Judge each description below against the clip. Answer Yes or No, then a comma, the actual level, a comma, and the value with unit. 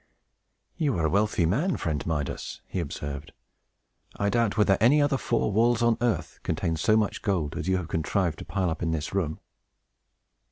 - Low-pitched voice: Yes, very low, 95 Hz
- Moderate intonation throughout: No, wide, 5.9 semitones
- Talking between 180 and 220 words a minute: Yes, average, 185 wpm